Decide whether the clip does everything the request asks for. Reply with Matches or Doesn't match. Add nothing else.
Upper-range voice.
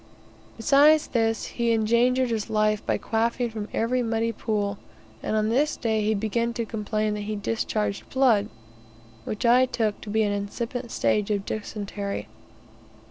Matches